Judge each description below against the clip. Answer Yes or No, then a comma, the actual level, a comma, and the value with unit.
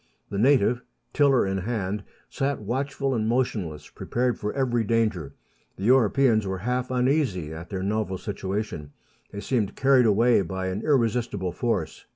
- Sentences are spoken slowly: No, average, 150 wpm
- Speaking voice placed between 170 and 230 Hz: No, low, 110 Hz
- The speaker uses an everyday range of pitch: Yes, average, 4.7 semitones